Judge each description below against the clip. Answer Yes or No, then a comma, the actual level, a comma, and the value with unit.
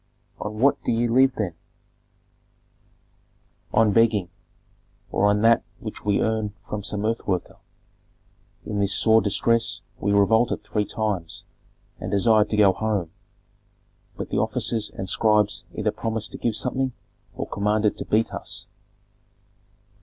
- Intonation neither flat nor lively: No, narrow, 1.8 semitones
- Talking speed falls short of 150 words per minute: Yes, average, 140 wpm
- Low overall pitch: Yes, low, 105 Hz